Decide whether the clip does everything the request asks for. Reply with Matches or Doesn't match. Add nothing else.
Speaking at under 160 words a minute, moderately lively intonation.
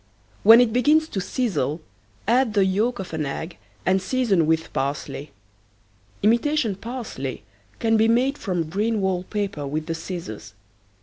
Doesn't match